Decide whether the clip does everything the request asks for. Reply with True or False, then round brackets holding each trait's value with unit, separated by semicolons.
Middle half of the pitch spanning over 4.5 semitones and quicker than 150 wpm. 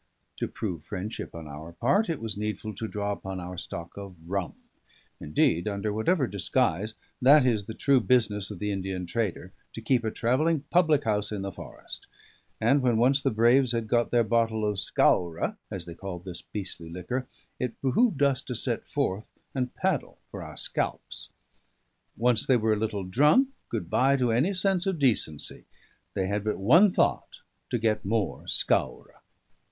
True (4.9 semitones; 180 wpm)